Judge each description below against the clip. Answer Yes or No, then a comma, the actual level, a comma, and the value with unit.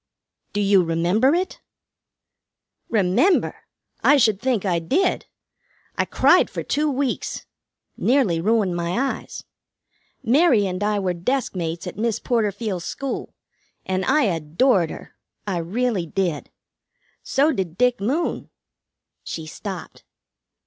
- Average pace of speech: No, slow, 120 wpm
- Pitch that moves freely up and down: Yes, wide, 6.4 semitones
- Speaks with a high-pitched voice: Yes, high, 205 Hz